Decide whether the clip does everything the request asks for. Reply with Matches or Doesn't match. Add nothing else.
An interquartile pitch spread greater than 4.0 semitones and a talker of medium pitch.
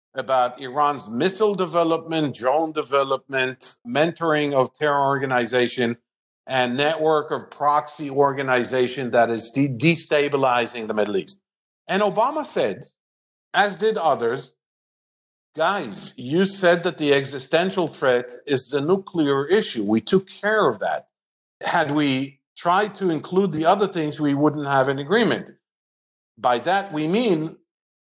Matches